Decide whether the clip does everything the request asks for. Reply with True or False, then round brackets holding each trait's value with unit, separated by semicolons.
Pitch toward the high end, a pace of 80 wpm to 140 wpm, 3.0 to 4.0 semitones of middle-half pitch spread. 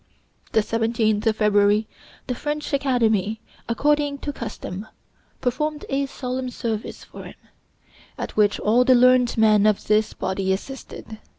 True (230 Hz; 135 wpm; 3.5 semitones)